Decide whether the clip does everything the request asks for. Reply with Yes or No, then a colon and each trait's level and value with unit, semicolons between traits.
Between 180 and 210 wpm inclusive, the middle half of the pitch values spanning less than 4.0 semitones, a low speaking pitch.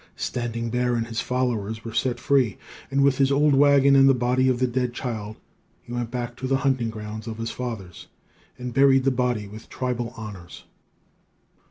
Yes: average, 190 wpm; narrow, 2.4 semitones; low, 125 Hz